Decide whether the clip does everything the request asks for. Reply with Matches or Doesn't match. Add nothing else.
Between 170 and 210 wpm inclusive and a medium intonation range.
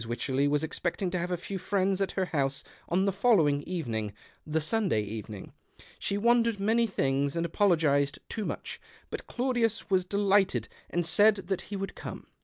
Doesn't match